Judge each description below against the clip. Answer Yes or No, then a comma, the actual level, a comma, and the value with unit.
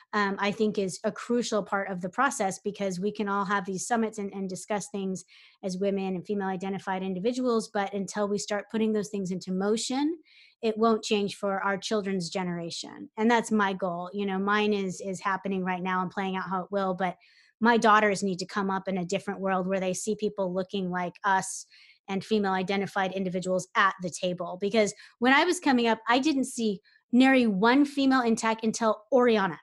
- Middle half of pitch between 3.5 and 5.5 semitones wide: No, narrow, 2.5 semitones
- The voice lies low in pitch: No, high, 200 Hz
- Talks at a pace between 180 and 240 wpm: Yes, fast, 205 wpm